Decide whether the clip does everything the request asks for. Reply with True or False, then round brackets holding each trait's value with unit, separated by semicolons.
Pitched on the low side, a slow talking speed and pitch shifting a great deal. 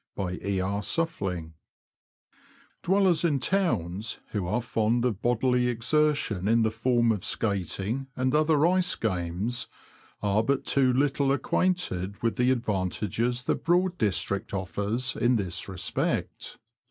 True (115 Hz; 130 wpm; 5.7 semitones)